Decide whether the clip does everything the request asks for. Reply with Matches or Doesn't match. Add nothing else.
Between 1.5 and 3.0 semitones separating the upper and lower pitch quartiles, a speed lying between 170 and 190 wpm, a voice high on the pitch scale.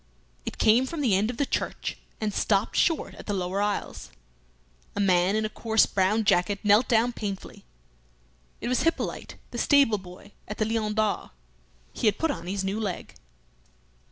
Matches